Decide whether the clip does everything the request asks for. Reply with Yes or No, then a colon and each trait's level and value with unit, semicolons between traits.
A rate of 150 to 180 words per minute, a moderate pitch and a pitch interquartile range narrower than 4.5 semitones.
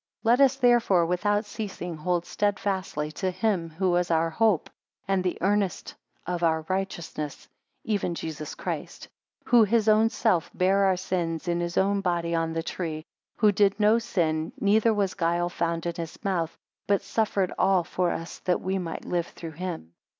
Yes: average, 175 wpm; medium, 180 Hz; average, 3.5 semitones